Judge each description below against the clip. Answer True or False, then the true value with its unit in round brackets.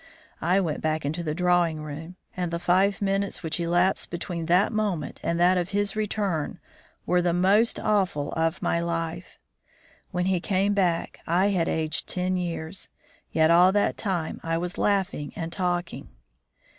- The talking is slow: False (165 wpm)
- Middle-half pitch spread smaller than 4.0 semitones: True (2.5 semitones)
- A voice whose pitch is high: False (175 Hz)